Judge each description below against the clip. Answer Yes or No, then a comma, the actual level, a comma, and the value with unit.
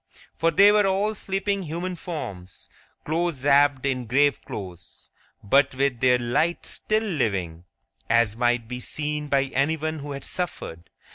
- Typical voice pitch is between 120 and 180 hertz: Yes, medium, 140 Hz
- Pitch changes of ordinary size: No, wide, 5.8 semitones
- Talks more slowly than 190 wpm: Yes, average, 145 wpm